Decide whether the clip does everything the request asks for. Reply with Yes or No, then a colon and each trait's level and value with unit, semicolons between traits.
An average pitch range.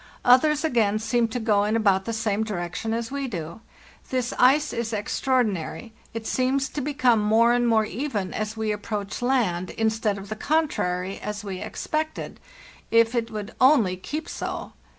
Yes: average, 3.5 semitones